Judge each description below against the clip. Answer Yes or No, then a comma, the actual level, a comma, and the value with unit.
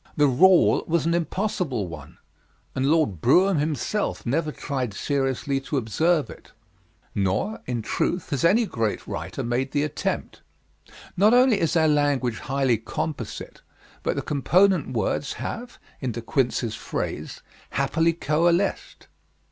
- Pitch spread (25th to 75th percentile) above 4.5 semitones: Yes, average, 5.2 semitones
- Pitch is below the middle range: No, medium, 145 Hz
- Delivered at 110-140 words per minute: Yes, slow, 135 wpm